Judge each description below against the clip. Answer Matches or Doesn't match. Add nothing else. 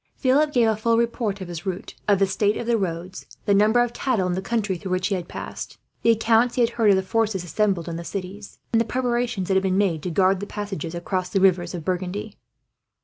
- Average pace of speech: Doesn't match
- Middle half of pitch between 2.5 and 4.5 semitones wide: Matches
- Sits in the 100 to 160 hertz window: Doesn't match